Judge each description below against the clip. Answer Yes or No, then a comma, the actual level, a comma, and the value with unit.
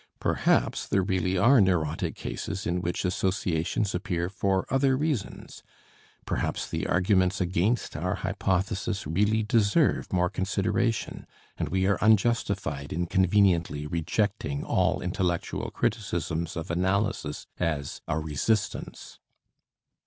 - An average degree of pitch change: Yes, average, 3.1 semitones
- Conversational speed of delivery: No, slow, 115 wpm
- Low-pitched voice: Yes, very low, 95 Hz